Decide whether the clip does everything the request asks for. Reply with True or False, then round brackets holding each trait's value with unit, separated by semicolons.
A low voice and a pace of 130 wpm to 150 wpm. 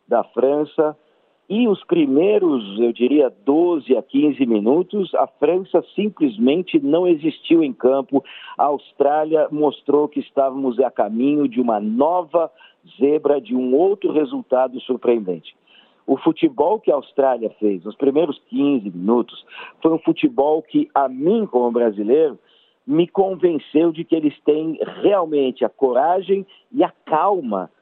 False (155 Hz; 140 wpm)